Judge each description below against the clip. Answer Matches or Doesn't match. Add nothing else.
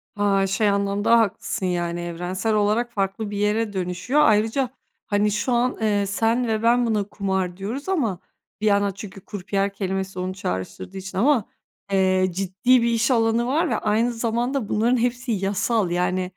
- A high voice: Matches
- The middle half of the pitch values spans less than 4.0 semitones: Matches